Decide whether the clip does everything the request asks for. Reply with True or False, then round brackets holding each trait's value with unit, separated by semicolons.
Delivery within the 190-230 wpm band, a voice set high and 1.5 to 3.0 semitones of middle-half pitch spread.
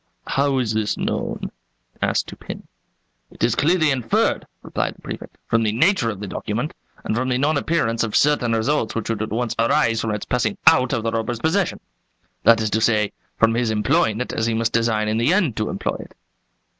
False (205 wpm; 115 Hz; 2.7 semitones)